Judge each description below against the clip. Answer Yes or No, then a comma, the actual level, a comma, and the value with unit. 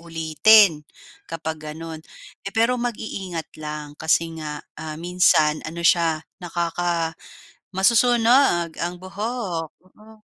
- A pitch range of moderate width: Yes, average, 4.3 semitones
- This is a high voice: No, medium, 170 Hz